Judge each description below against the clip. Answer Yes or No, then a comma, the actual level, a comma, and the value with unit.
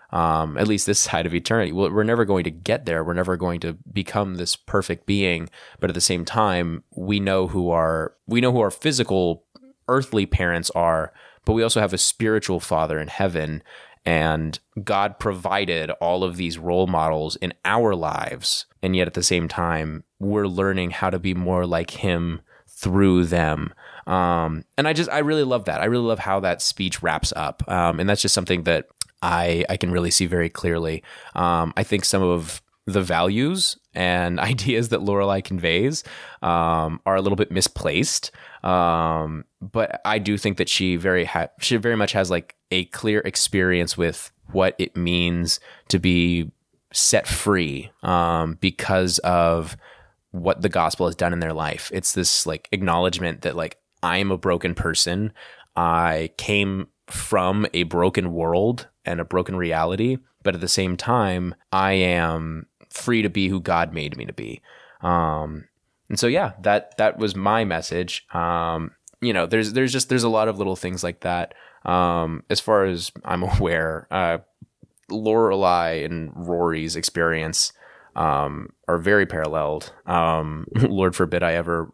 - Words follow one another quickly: No, average, 175 wpm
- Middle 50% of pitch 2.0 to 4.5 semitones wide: Yes, average, 2.9 semitones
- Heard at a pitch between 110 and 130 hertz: No, very low, 90 Hz